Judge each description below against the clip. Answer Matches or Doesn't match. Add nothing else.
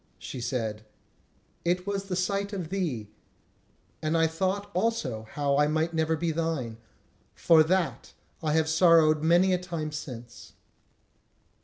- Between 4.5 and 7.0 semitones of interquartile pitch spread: Doesn't match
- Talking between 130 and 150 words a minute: Matches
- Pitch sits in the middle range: Matches